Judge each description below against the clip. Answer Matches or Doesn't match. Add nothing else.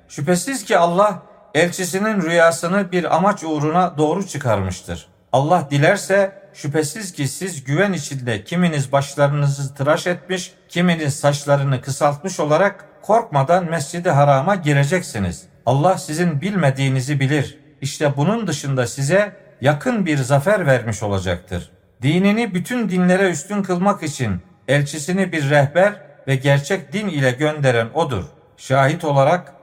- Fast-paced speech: Doesn't match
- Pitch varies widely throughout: Doesn't match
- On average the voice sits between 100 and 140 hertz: Doesn't match